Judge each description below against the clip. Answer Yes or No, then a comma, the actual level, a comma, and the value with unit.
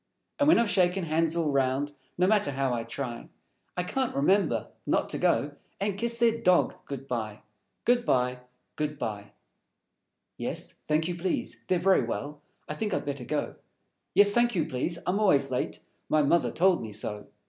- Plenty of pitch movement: Yes, wide, 6.2 semitones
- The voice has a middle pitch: Yes, medium, 160 Hz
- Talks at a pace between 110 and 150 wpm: No, average, 180 wpm